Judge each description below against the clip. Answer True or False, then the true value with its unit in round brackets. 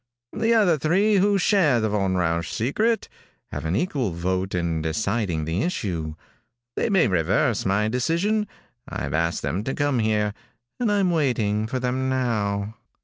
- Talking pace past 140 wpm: True (155 wpm)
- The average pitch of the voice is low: True (110 Hz)